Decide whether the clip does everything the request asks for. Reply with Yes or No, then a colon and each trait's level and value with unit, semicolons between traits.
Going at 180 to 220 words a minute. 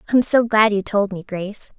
No: fast, 270 wpm